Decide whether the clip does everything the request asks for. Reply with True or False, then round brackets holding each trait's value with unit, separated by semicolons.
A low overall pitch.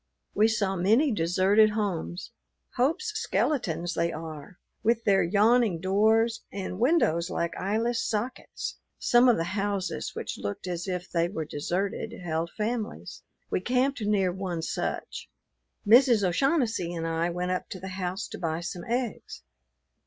False (195 Hz)